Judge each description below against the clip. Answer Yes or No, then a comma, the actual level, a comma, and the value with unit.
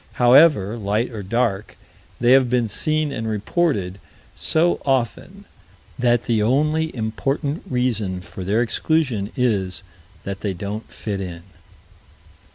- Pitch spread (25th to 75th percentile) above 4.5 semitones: Yes, average, 5.1 semitones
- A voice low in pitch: Yes, low, 115 Hz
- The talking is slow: Yes, slow, 125 wpm